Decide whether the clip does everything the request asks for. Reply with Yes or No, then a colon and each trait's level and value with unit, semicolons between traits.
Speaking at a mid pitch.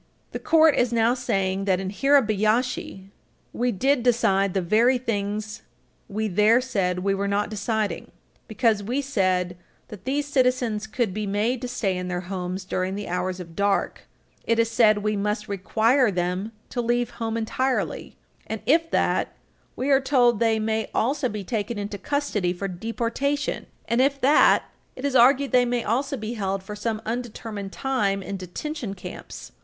No: high, 220 Hz